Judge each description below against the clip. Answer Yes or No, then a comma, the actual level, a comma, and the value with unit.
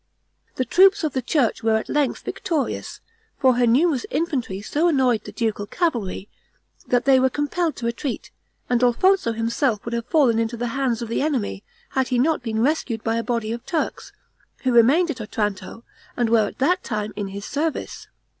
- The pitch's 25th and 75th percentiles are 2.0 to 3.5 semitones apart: No, average, 4.3 semitones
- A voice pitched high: Yes, high, 245 Hz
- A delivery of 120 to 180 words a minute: No, average, 190 wpm